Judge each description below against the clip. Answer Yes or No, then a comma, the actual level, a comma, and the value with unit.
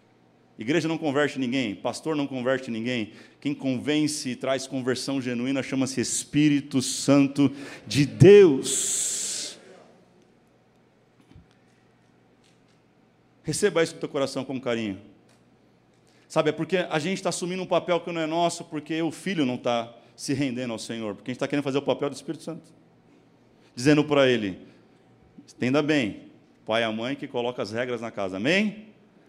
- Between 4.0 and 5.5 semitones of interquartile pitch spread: Yes, average, 4.7 semitones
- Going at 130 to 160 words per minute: Yes, average, 150 wpm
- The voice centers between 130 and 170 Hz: Yes, medium, 140 Hz